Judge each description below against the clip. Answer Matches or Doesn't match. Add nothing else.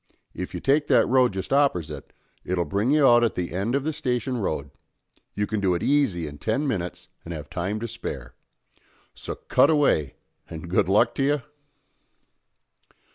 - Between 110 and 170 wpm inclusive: Doesn't match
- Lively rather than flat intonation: Matches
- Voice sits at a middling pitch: Doesn't match